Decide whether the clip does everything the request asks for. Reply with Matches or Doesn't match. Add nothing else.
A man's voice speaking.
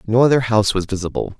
Matches